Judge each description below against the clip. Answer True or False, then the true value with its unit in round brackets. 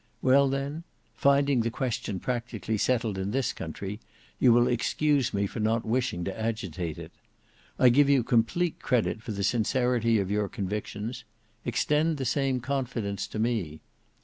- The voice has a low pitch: True (120 Hz)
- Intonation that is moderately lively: True (4.1 semitones)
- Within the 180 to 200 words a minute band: False (155 wpm)